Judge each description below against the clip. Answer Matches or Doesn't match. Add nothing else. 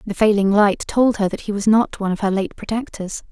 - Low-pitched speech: Doesn't match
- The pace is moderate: Doesn't match